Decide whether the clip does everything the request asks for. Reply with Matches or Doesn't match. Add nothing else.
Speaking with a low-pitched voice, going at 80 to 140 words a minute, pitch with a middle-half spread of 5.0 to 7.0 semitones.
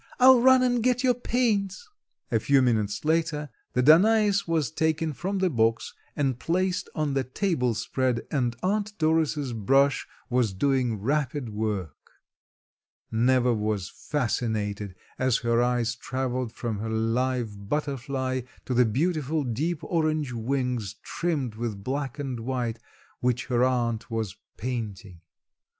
Matches